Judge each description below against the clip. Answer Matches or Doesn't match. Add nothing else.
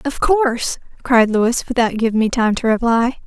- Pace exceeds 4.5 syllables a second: Matches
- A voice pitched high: Matches